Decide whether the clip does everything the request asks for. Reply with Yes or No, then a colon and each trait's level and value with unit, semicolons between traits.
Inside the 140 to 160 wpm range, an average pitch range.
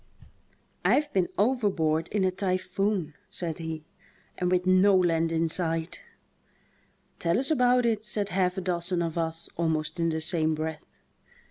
Yes: average, 150 wpm; average, 3.2 semitones